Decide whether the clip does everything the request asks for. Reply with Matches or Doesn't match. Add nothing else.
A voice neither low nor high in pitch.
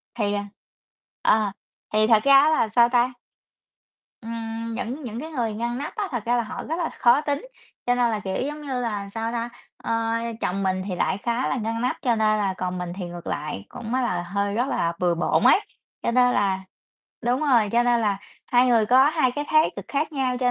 Doesn't match